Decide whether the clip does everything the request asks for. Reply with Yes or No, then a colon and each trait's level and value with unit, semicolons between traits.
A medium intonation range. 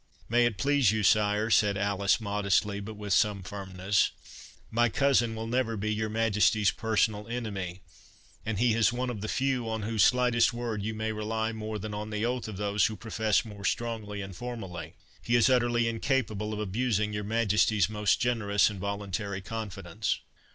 No: narrow, 2.2 semitones